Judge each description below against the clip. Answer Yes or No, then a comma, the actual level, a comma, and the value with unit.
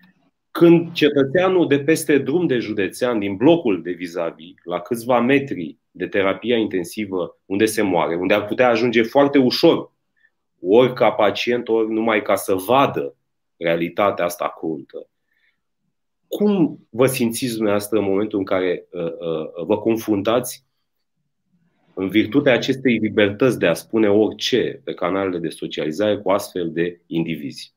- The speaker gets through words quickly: No, average, 140 wpm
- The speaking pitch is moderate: No, low, 115 Hz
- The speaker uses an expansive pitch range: Yes, wide, 5.8 semitones